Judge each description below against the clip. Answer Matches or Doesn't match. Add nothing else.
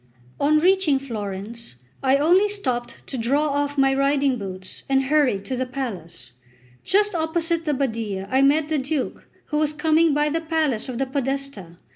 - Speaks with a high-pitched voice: Matches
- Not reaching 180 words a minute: Matches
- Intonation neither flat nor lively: Matches